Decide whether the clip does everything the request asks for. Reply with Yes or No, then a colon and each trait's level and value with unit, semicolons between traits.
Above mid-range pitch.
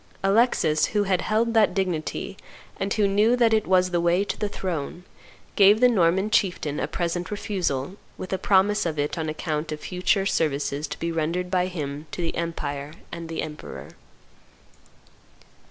No: medium, 180 Hz